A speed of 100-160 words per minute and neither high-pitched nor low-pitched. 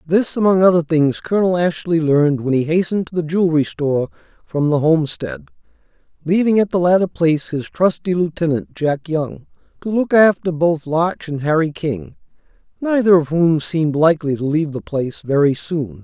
No: average, 170 wpm; medium, 160 Hz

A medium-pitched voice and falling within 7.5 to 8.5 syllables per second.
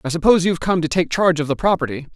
Yes: medium, 165 Hz; 8.0 syllables/s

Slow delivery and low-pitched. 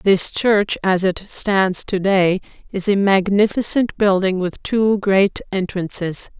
No: slow, 130 wpm; high, 195 Hz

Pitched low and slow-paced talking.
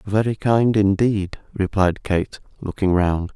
Yes: low, 100 Hz; slow, 125 wpm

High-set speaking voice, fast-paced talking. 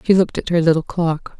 No: medium, 170 Hz; fast, 260 wpm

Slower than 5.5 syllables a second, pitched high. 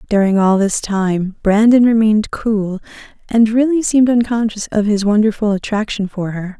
Yes: 5.0 syllables/s; high, 215 Hz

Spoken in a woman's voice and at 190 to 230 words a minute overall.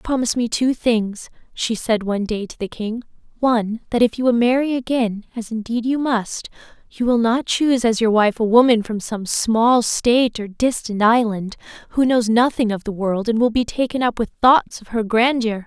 Yes: female; fast, 205 wpm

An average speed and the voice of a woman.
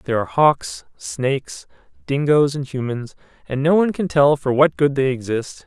No: average, 180 wpm; male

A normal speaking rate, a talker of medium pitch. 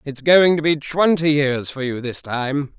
No: fast, 215 wpm; medium, 145 Hz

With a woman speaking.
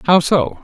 No: male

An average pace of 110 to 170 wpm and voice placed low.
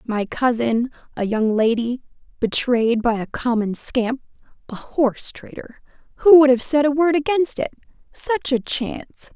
No: average, 140 wpm; very high, 255 Hz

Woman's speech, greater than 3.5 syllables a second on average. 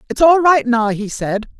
Yes: female; 4.6 syllables/s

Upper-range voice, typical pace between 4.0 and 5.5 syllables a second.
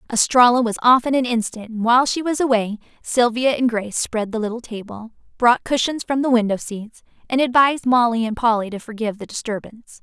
No: high, 235 Hz; 5.9 syllables/s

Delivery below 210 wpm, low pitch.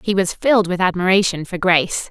No: average, 200 wpm; medium, 185 Hz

